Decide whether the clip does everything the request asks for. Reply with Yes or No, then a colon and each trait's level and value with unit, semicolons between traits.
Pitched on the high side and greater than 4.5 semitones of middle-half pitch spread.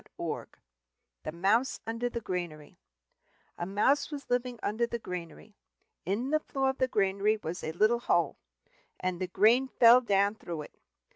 Yes: high, 215 Hz; average, 5.1 semitones